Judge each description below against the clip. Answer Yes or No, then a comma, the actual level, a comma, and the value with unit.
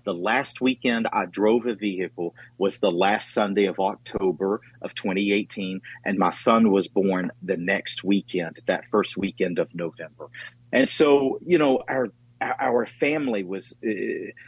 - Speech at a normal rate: Yes, average, 155 wpm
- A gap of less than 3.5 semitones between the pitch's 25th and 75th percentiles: No, average, 4.0 semitones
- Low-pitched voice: Yes, low, 105 Hz